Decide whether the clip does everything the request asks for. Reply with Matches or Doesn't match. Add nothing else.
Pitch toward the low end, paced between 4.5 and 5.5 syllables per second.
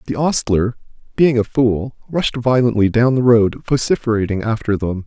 Matches